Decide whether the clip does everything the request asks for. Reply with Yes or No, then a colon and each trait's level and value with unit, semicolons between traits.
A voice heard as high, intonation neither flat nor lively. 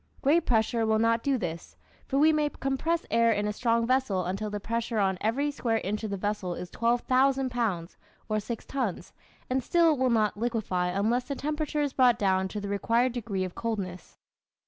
Yes: high, 230 Hz; average, 4.3 semitones